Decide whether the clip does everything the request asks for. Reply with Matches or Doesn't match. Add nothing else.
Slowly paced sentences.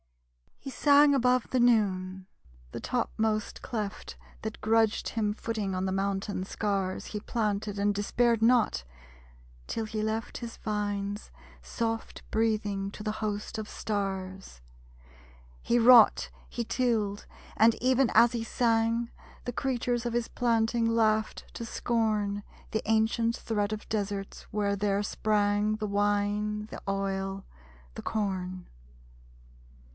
Matches